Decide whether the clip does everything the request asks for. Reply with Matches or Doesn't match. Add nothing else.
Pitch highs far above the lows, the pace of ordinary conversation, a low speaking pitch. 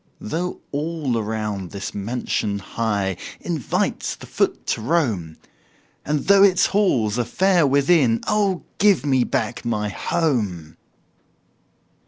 Doesn't match